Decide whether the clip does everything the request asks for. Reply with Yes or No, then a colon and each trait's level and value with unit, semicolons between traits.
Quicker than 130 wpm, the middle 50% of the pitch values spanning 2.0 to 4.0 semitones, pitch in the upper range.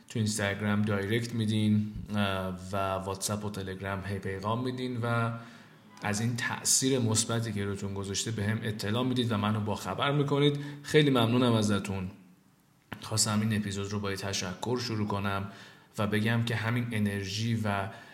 No: average, 150 wpm; narrow, 2.6 semitones; low, 105 Hz